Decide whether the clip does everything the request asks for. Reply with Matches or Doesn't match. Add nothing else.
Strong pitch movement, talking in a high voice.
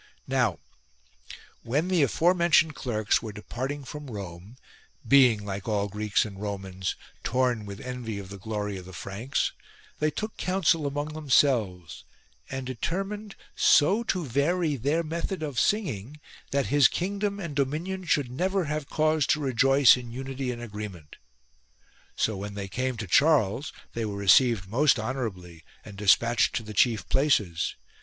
Doesn't match